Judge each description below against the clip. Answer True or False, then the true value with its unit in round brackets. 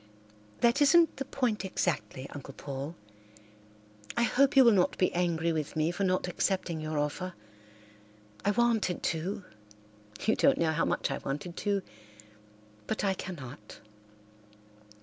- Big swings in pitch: True (6.8 semitones)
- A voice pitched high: False (170 Hz)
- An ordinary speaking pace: False (130 wpm)